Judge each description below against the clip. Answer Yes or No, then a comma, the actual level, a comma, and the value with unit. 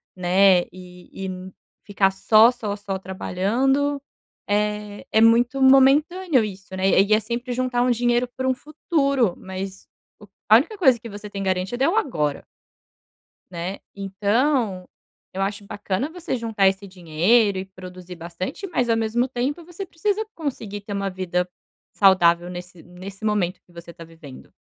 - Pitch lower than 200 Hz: No, high, 205 Hz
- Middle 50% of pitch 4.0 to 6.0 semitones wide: Yes, average, 5.1 semitones